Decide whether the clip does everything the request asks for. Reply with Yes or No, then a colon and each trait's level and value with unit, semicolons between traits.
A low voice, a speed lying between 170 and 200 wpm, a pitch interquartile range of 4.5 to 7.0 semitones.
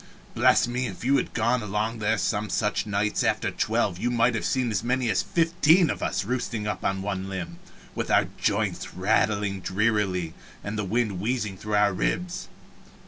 No: low, 105 Hz; average, 180 wpm; average, 3.6 semitones